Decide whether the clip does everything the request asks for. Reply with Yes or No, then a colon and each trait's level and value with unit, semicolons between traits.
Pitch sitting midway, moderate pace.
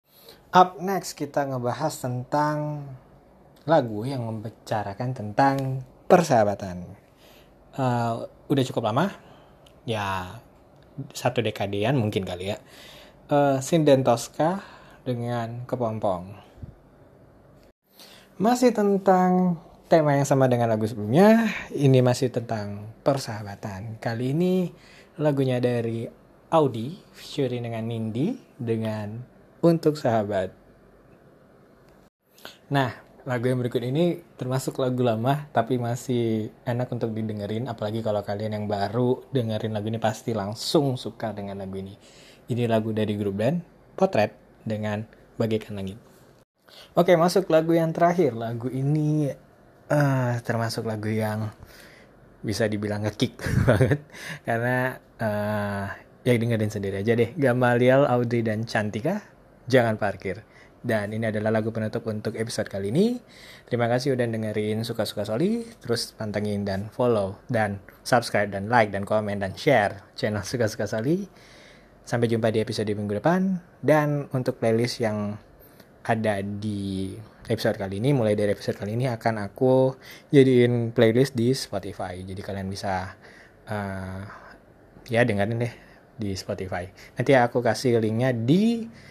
No: low, 120 Hz; average, 120 wpm